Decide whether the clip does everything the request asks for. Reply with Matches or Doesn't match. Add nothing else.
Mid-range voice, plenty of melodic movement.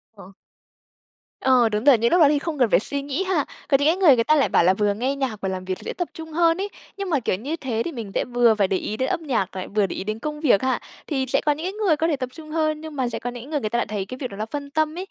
Doesn't match